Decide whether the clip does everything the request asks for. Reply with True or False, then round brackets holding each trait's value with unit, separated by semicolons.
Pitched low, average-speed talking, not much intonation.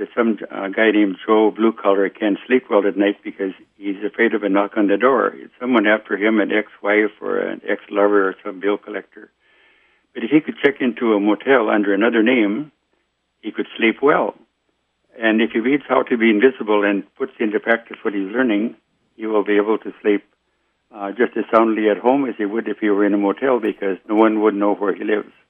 False (105 Hz; 225 wpm; 2.1 semitones)